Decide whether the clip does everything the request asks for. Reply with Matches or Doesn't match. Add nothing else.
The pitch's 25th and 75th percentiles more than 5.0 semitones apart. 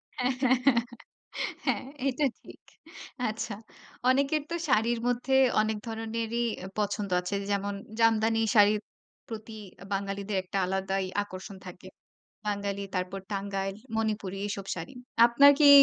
Doesn't match